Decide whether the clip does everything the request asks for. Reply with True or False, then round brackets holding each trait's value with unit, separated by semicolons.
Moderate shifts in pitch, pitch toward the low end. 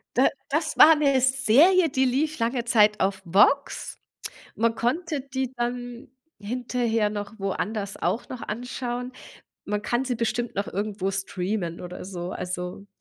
False (4.3 semitones; 235 Hz)